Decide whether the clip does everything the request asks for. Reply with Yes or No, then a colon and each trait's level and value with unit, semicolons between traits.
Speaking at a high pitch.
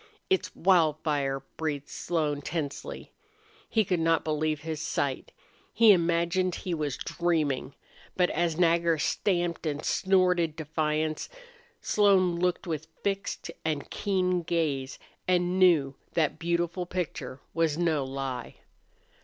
No: medium, 165 Hz